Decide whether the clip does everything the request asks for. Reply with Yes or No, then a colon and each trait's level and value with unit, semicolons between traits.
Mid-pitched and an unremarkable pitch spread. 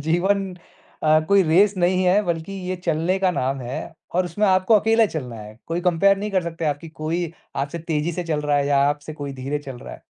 Yes: medium, 165 Hz; average, 4.0 semitones